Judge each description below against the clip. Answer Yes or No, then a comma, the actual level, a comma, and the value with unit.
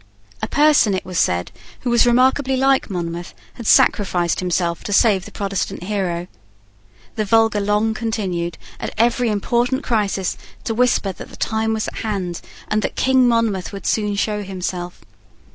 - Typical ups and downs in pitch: Yes, average, 3.9 semitones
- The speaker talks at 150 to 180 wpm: Yes, average, 160 wpm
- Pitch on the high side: Yes, high, 210 Hz